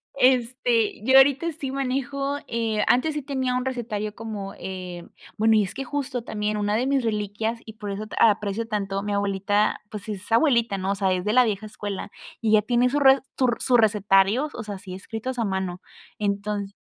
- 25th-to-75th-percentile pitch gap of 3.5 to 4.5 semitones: Yes, average, 3.8 semitones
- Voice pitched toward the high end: Yes, high, 220 Hz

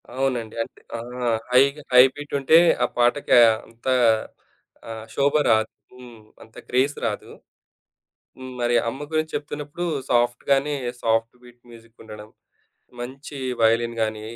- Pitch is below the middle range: Yes, low, 125 Hz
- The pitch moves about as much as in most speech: Yes, average, 3.4 semitones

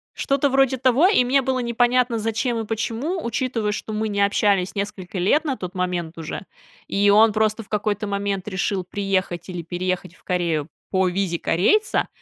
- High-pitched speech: Yes, high, 205 Hz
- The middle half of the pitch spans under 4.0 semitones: No, average, 4.7 semitones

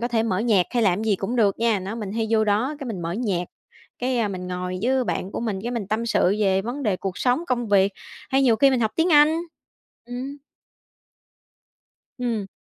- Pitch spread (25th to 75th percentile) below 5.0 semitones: Yes, average, 4.0 semitones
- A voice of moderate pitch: No, high, 225 Hz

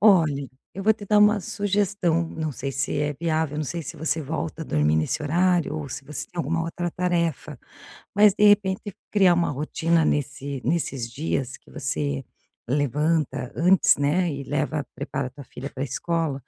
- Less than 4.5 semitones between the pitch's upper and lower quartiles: Yes, average, 3.9 semitones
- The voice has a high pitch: No, medium, 160 Hz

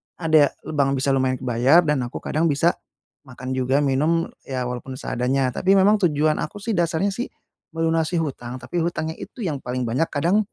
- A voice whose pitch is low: No, medium, 150 Hz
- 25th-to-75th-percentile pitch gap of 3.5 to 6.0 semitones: Yes, average, 4.3 semitones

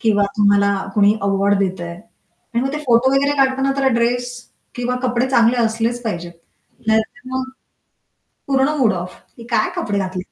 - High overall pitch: Yes, high, 230 Hz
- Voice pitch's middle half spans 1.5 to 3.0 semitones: No, average, 4.4 semitones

